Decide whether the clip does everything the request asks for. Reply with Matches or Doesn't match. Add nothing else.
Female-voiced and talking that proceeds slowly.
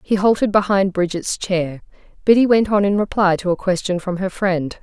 Doesn't match